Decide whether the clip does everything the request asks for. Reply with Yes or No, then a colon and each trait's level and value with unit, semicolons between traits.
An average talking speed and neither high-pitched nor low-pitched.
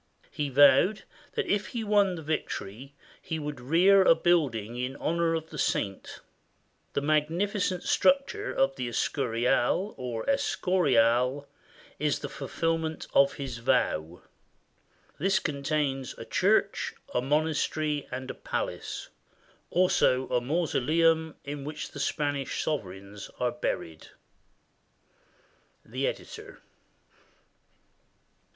No: slow, 110 wpm; medium, 145 Hz